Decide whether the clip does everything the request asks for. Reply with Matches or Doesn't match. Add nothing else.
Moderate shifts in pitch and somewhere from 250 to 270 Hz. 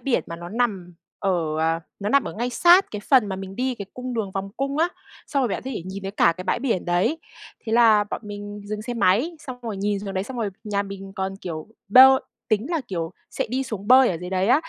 Doesn't match